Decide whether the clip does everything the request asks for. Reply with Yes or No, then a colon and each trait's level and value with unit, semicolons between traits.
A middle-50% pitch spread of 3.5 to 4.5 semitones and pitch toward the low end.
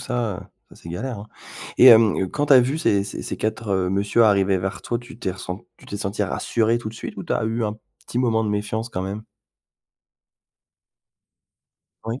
No: average, 3.1 semitones; low, 110 Hz